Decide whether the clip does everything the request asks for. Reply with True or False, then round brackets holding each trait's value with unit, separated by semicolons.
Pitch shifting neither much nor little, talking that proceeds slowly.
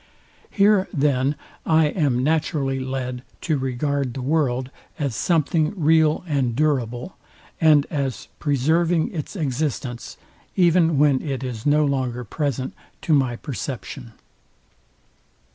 True (3.4 semitones; 115 wpm)